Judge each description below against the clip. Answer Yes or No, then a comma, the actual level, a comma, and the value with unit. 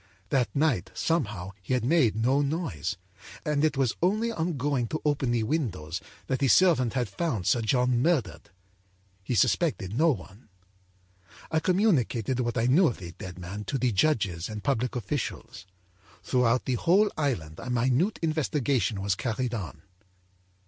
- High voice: No, low, 125 Hz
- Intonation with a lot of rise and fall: Yes, wide, 6.1 semitones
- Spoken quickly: No, average, 160 wpm